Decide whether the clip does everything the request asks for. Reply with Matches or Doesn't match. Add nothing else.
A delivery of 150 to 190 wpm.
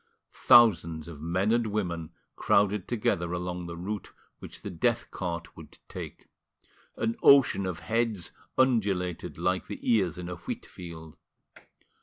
Doesn't match